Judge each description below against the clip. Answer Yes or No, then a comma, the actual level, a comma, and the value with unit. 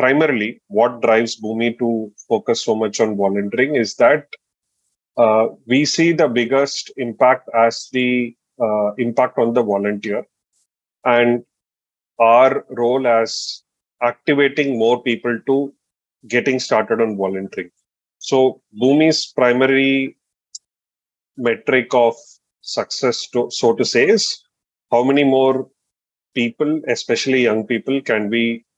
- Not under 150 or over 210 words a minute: No, average, 120 wpm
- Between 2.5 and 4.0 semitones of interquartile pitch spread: Yes, average, 2.9 semitones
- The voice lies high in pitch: No, low, 120 Hz